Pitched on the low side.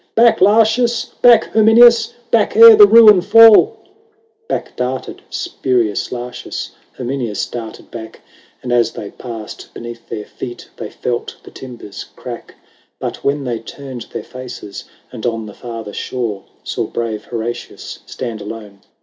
Yes: low, 125 Hz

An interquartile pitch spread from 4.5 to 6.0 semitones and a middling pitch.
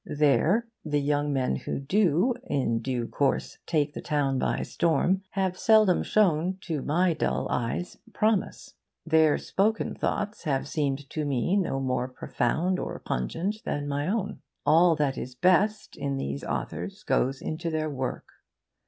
Yes: average, 5.2 semitones; medium, 150 Hz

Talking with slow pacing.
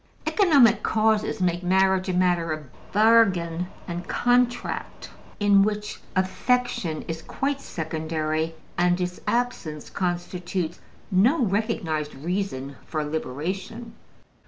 Yes: slow, 105 wpm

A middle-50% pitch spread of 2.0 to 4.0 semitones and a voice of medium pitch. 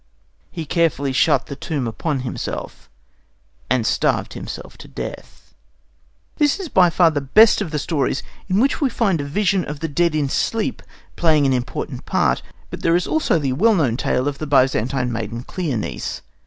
No: average, 5.2 semitones; medium, 150 Hz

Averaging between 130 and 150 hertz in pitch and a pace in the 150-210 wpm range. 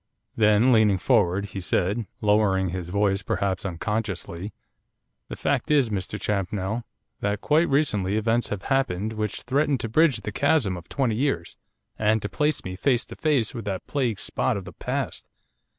No: low, 105 Hz; average, 165 wpm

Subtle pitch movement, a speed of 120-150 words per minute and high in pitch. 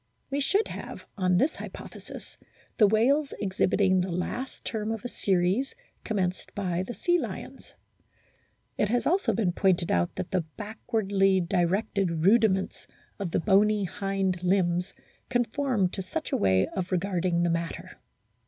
No: average, 3.5 semitones; average, 145 wpm; high, 195 Hz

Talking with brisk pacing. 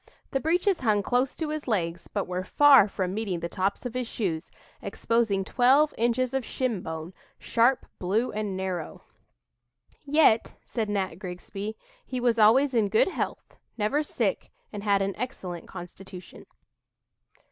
No: average, 145 wpm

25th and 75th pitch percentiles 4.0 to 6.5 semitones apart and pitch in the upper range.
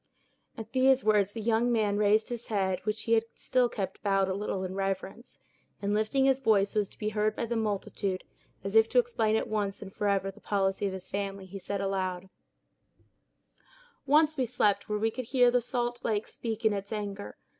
No: average, 2.7 semitones; high, 210 Hz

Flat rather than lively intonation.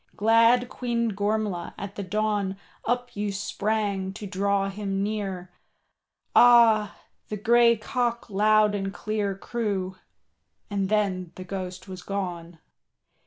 Yes: narrow, 2.1 semitones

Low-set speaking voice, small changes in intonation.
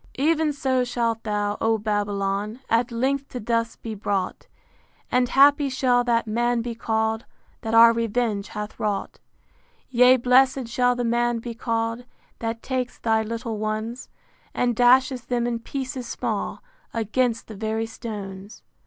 No: high, 230 Hz; narrow, 2.1 semitones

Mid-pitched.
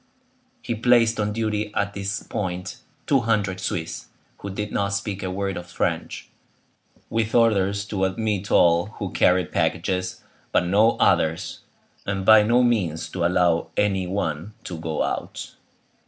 No: low, 100 Hz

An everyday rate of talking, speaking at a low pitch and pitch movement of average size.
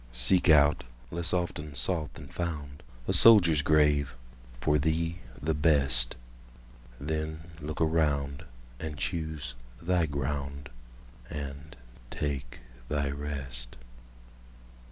No: slow, 85 wpm; very low, 75 Hz; average, 3.3 semitones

